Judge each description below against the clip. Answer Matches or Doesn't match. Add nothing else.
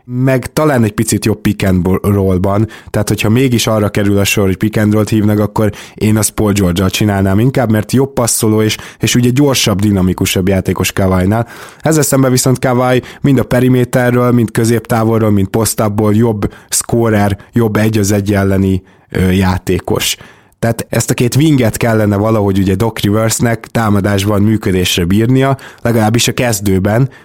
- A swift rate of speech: Matches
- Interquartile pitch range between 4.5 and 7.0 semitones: Doesn't match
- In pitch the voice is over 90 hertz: Matches